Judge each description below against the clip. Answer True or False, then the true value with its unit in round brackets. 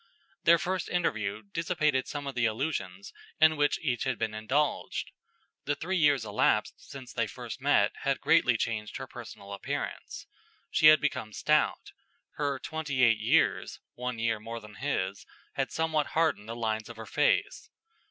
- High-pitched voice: False (130 Hz)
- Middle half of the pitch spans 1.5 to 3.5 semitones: False (5.3 semitones)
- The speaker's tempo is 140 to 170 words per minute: True (160 wpm)